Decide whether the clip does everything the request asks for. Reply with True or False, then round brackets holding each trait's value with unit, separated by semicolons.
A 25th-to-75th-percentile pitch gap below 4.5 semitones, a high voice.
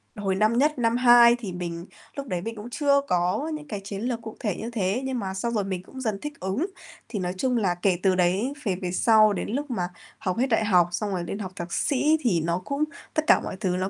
False (4.9 semitones; 210 Hz)